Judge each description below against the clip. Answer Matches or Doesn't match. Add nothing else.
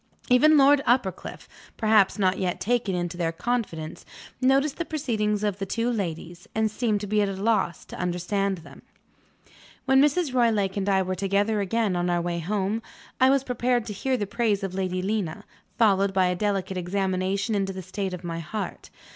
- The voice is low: Doesn't match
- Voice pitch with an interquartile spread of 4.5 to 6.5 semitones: Doesn't match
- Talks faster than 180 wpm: Matches